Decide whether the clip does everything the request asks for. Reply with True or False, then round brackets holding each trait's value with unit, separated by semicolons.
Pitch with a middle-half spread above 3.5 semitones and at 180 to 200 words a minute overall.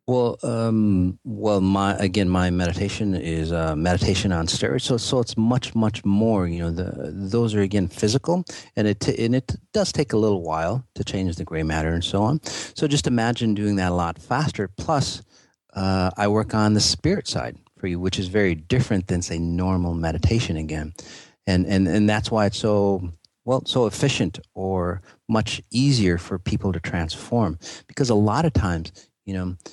True (3.9 semitones; 190 wpm)